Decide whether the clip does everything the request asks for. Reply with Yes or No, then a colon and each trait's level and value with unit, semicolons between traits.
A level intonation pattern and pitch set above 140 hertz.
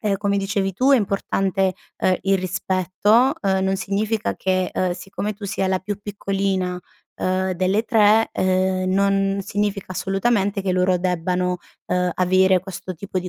Yes: narrow, 1.4 semitones; high, 190 Hz